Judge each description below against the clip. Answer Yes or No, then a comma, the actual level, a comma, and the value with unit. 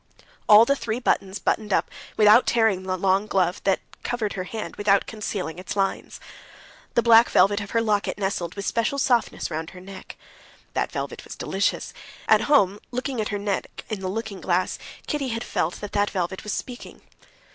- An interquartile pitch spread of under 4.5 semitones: Yes, average, 3.0 semitones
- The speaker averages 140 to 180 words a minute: No, average, 190 wpm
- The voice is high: Yes, high, 205 Hz